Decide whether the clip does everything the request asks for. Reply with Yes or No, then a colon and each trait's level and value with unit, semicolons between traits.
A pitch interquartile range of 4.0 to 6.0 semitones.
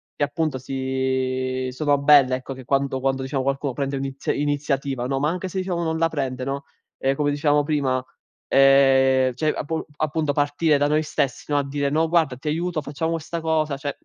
No: narrow, 2.4 semitones